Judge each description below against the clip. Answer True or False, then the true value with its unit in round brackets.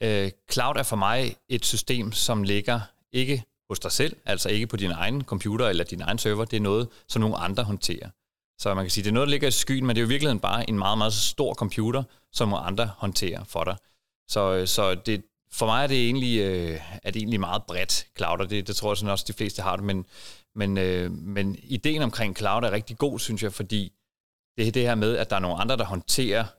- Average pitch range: True (3.1 semitones)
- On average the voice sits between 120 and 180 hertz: False (105 Hz)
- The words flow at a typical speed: False (255 wpm)